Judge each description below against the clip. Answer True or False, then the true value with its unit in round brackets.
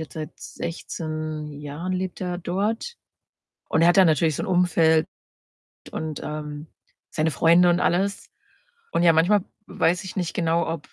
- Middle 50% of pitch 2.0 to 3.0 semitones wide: True (2.4 semitones)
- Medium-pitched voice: True (165 Hz)